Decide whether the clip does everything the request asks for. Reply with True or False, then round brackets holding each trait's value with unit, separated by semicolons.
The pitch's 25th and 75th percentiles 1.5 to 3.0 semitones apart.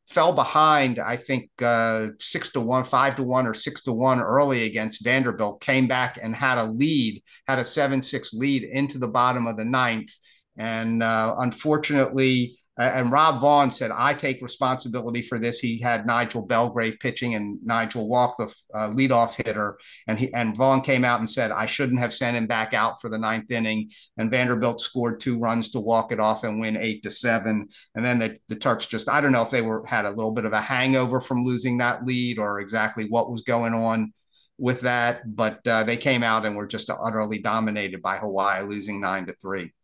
True (2.4 semitones)